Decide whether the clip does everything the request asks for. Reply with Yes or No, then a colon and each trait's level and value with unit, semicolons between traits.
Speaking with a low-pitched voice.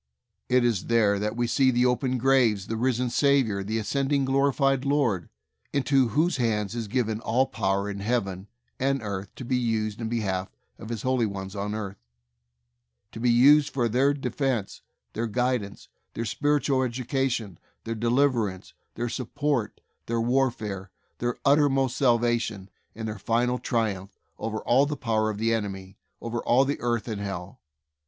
Yes: low, 115 Hz